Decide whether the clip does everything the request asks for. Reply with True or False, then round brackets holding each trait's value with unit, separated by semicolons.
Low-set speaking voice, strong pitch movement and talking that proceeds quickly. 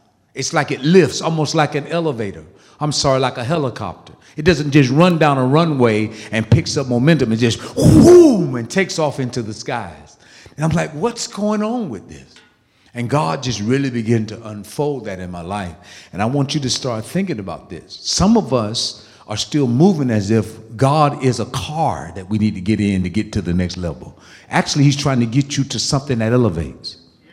True (130 Hz; 5.7 semitones; 210 wpm)